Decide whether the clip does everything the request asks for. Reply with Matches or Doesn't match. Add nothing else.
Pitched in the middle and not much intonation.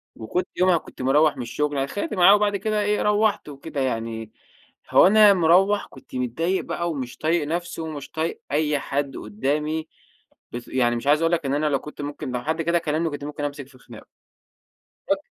Doesn't match